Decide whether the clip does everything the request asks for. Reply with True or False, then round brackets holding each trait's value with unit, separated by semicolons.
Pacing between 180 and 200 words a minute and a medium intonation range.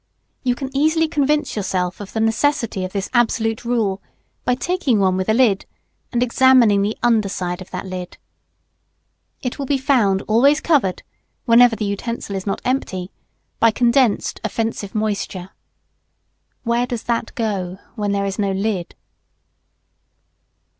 False (145 wpm; 4.2 semitones)